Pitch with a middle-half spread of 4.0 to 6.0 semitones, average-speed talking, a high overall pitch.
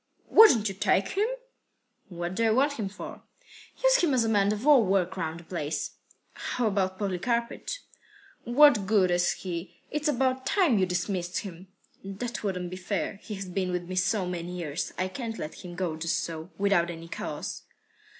Yes: average, 4.5 semitones; average, 180 wpm; high, 195 Hz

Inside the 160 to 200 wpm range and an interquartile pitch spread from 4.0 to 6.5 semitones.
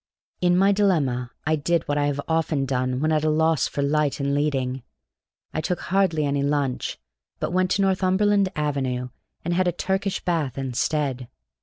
Yes: average, 175 wpm; average, 4.3 semitones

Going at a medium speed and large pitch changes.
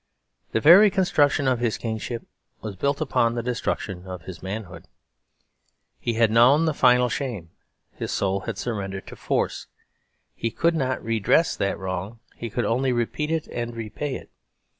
No: average, 160 wpm; average, 4.8 semitones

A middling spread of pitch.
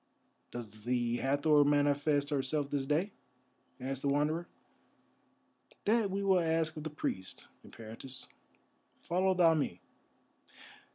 Yes: average, 3.4 semitones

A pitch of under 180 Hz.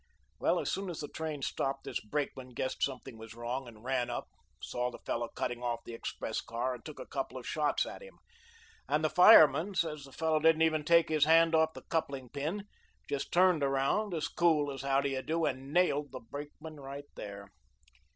Yes: medium, 140 Hz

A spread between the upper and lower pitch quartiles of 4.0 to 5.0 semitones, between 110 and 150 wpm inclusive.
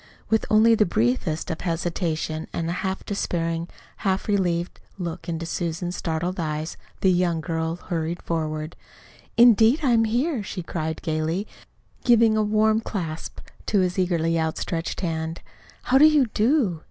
Yes: average, 4.6 semitones; average, 145 wpm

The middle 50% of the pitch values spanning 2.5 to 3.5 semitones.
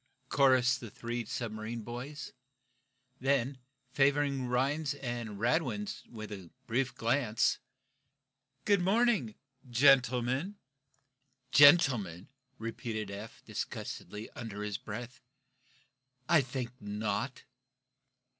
No: average, 4.0 semitones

